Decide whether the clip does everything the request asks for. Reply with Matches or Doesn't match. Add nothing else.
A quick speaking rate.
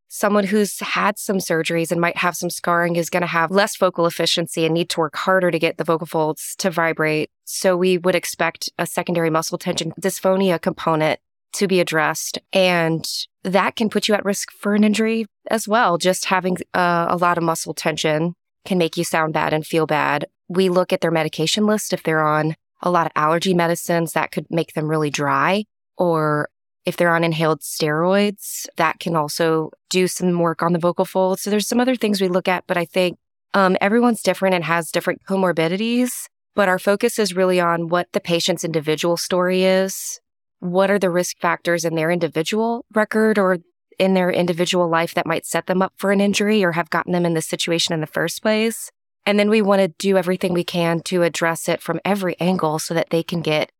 Matches